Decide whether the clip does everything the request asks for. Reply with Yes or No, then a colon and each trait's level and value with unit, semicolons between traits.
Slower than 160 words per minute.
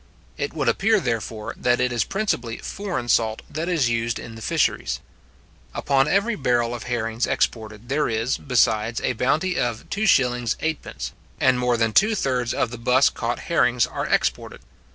No: average, 165 wpm